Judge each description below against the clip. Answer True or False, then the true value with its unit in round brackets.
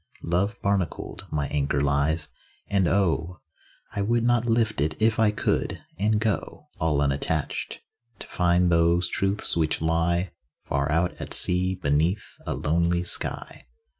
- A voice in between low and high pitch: False (85 Hz)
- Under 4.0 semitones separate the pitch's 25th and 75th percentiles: False (4.3 semitones)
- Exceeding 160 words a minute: False (140 wpm)